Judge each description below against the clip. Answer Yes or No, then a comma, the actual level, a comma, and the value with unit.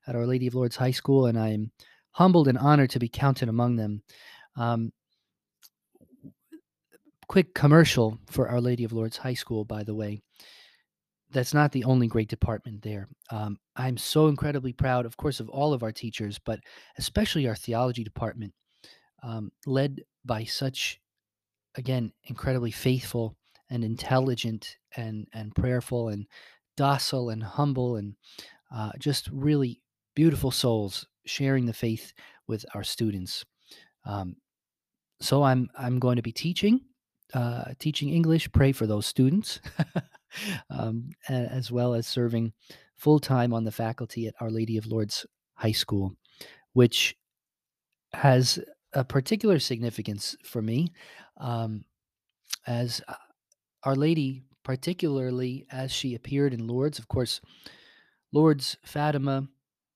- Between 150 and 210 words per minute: No, slow, 135 wpm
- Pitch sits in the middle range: No, low, 125 Hz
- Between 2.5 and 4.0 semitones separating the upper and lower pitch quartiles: Yes, average, 3.6 semitones